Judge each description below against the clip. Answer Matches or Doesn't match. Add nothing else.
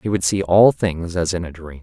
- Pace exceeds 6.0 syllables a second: Doesn't match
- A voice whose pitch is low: Matches